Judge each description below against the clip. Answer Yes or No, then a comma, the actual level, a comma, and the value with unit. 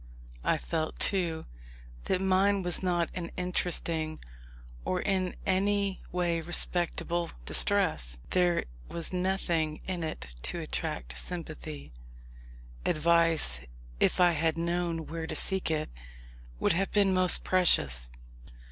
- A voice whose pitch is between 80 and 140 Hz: No, medium, 170 Hz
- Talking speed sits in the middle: No, slow, 120 wpm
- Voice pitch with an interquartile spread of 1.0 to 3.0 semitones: Yes, narrow, 2.5 semitones